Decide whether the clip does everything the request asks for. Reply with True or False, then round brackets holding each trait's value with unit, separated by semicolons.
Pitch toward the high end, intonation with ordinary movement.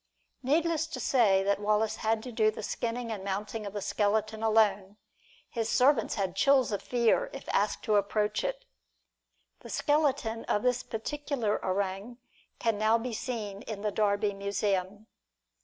True (220 Hz; 3.3 semitones)